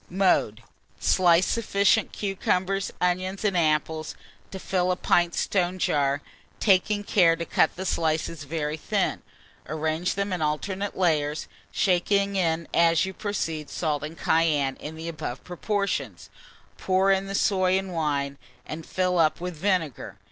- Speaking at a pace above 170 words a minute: No, average, 145 wpm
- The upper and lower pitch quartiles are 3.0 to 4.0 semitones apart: Yes, average, 3.4 semitones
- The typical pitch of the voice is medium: Yes, medium, 175 Hz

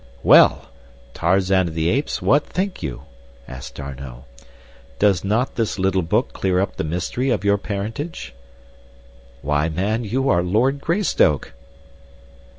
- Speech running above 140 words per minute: No, slow, 135 wpm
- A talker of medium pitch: No, very low, 95 Hz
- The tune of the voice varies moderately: No, wide, 6.6 semitones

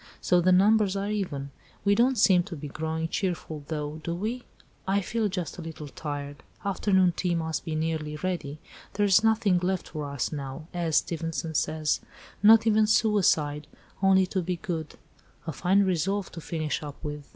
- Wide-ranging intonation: No, average, 4.3 semitones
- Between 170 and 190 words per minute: Yes, average, 175 wpm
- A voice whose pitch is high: No, medium, 175 Hz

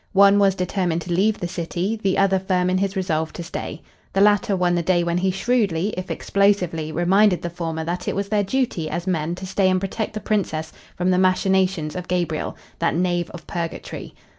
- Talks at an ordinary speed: No, fast, 210 wpm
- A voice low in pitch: No, medium, 185 Hz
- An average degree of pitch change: No, narrow, 2.3 semitones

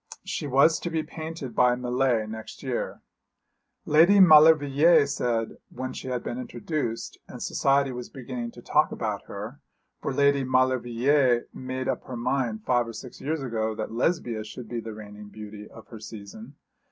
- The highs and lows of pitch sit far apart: No, average, 3.8 semitones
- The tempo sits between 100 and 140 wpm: No, average, 165 wpm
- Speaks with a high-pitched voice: No, low, 125 Hz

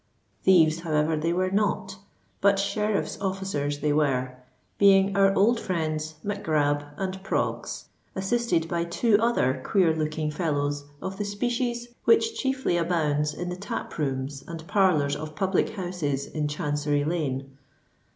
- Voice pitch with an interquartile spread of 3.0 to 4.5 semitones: No, average, 5.0 semitones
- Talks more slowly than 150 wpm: Yes, average, 140 wpm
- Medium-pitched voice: Yes, medium, 170 Hz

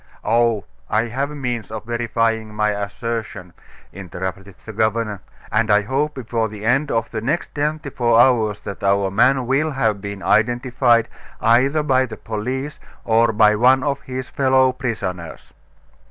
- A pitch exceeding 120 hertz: No, low, 115 Hz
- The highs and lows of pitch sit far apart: No, average, 3.5 semitones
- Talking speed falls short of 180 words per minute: Yes, average, 155 wpm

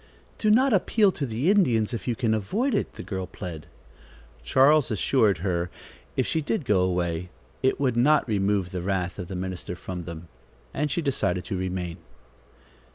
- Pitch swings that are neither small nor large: No, wide, 7.8 semitones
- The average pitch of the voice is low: Yes, low, 105 Hz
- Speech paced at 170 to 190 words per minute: Yes, average, 175 wpm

